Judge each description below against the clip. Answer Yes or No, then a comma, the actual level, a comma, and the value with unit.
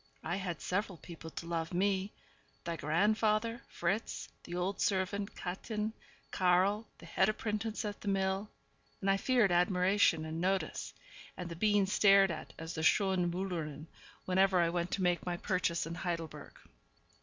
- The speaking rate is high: No, average, 155 wpm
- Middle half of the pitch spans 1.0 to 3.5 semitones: Yes, average, 2.8 semitones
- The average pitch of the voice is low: No, medium, 185 Hz